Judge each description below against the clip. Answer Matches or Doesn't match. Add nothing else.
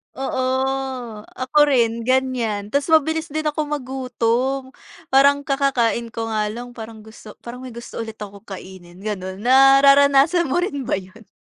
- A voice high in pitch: Matches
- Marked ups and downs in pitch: Doesn't match